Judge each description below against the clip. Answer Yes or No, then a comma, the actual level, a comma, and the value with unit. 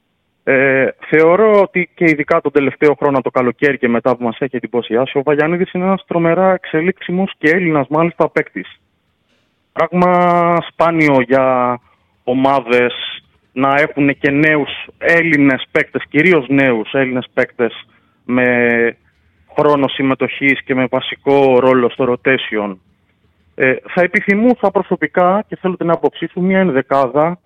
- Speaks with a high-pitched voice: No, medium, 140 Hz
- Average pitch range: Yes, average, 4.8 semitones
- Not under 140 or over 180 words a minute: No, average, 130 wpm